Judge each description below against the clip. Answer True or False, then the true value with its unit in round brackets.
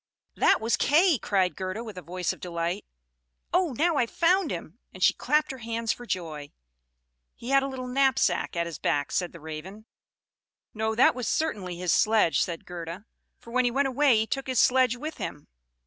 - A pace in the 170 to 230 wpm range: True (195 wpm)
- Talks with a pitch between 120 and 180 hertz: False (220 Hz)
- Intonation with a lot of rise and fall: True (6.9 semitones)